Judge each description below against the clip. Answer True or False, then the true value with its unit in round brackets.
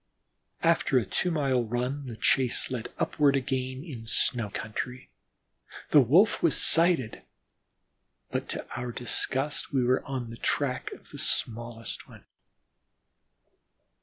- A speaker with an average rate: False (130 wpm)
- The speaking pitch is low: True (130 Hz)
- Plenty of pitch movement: False (2.9 semitones)